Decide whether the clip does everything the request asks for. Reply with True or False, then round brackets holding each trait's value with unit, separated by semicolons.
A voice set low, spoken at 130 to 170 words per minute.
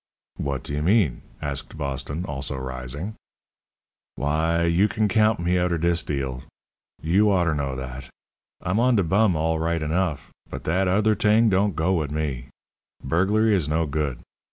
True (80 Hz; 160 wpm)